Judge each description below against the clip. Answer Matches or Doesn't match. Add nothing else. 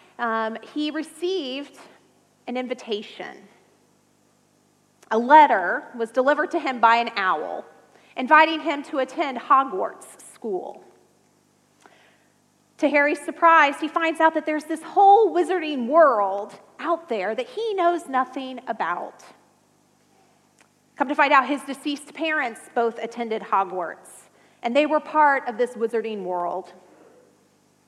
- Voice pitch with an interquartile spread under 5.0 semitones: Doesn't match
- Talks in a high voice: Matches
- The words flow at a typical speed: Doesn't match